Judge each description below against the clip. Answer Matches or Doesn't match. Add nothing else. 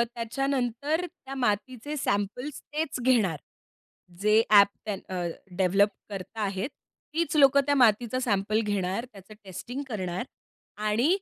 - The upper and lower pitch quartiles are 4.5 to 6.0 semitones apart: Matches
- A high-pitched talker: Matches